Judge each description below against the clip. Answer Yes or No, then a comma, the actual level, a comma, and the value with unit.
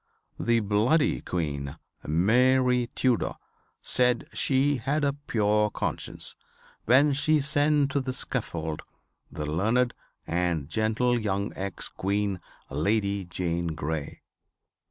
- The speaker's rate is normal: No, slow, 110 wpm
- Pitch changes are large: Yes, wide, 6.5 semitones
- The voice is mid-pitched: No, low, 110 Hz